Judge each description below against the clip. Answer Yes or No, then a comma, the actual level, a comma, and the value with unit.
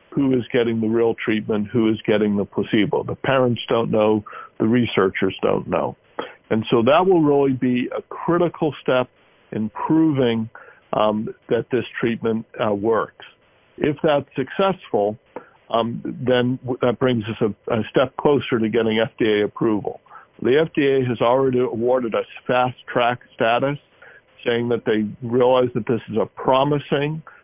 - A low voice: Yes, low, 125 Hz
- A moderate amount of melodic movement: Yes, average, 3.2 semitones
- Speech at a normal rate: Yes, average, 155 wpm